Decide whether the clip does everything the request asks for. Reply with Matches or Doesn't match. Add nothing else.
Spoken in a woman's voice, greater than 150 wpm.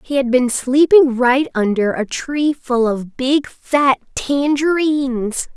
Doesn't match